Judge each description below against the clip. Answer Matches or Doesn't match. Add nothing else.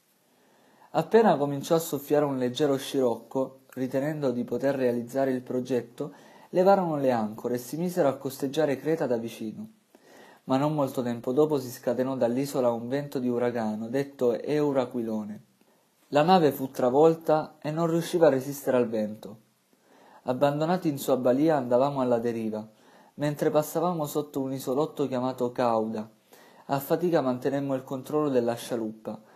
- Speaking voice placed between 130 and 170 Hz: Matches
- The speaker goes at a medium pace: Matches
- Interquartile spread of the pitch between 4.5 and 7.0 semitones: Doesn't match